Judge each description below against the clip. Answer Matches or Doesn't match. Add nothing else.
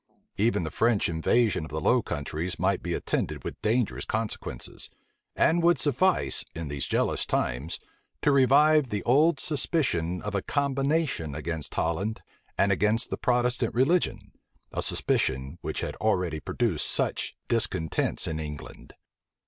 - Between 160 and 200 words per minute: Doesn't match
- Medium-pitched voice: Doesn't match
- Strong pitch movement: Matches